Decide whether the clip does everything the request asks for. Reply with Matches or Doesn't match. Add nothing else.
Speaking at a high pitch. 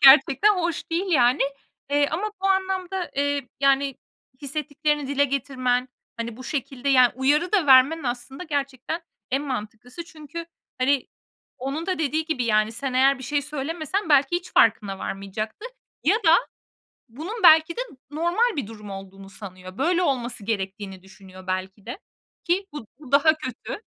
Matches